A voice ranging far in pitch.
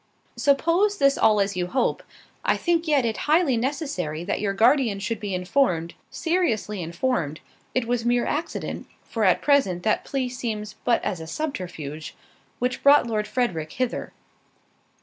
Yes: wide, 6.8 semitones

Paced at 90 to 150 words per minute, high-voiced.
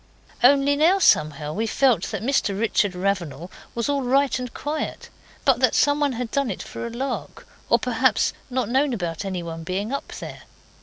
No: average, 185 wpm; high, 240 Hz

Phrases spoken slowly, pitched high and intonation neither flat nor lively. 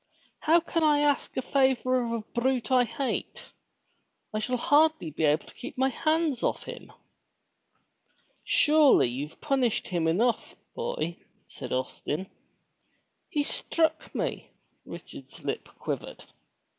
No: slow, 130 wpm; very high, 255 Hz; wide, 5.9 semitones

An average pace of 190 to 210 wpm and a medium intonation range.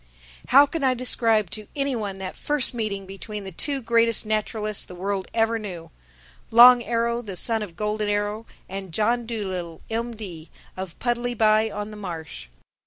No: average, 165 wpm; average, 3.2 semitones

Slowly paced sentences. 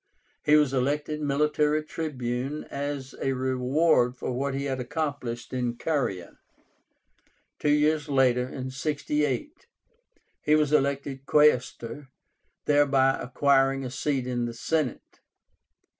Yes: slow, 115 wpm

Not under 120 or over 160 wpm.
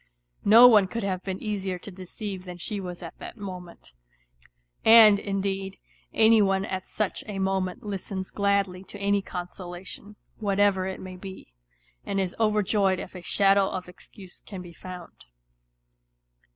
Yes: average, 150 wpm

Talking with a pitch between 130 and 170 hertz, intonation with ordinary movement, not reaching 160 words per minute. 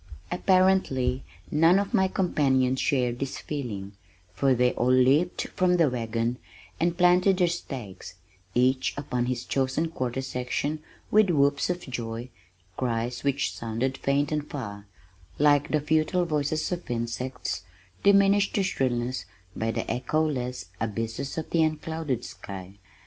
Yes: low, 135 Hz; average, 4.6 semitones; slow, 135 wpm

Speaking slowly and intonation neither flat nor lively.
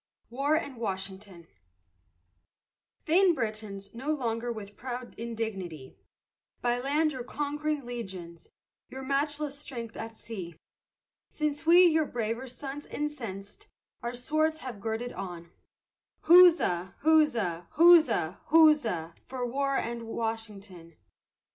No: slow, 110 wpm; wide, 6.5 semitones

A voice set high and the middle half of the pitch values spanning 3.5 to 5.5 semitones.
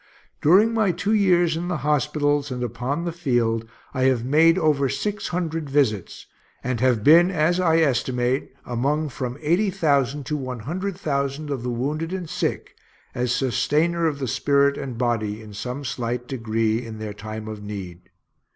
No: medium, 140 Hz; average, 5.1 semitones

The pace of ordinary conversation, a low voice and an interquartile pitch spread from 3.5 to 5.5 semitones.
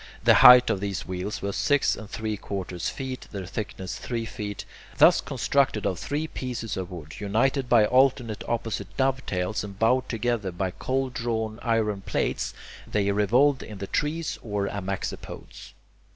Yes: average, 155 wpm; low, 110 Hz; average, 4.2 semitones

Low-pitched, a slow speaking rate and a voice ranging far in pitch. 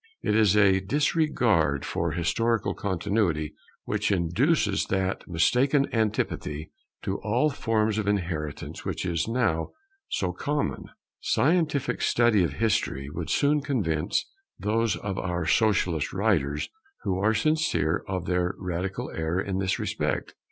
No: low, 100 Hz; slow, 130 wpm; average, 4.9 semitones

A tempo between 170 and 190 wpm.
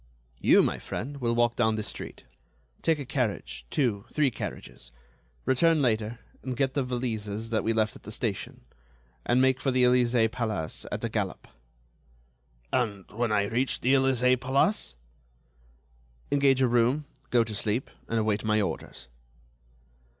No: average, 155 wpm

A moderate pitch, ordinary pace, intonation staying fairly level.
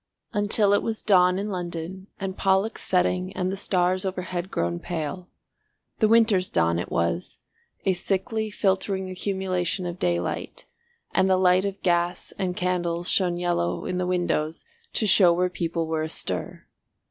Yes: medium, 180 Hz; average, 155 wpm; narrow, 1.8 semitones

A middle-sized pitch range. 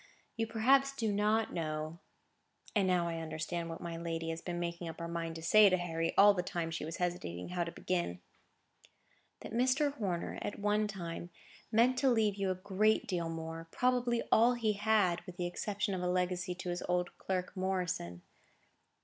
Yes: average, 3.9 semitones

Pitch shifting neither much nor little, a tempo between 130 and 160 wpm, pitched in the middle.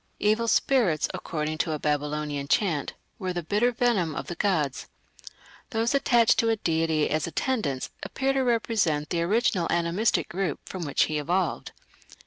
No: wide, 6.7 semitones; average, 155 wpm; medium, 175 Hz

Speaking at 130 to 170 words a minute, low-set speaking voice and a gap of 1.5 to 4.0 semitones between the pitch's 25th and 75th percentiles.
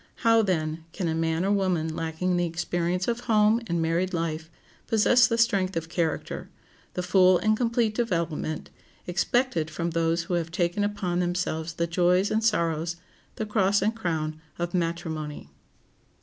No: average, 160 wpm; medium, 175 Hz; average, 3.7 semitones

